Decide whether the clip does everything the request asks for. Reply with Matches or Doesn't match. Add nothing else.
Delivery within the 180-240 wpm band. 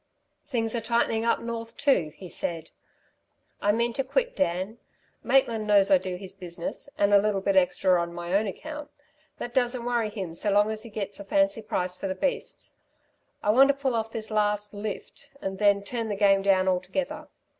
Matches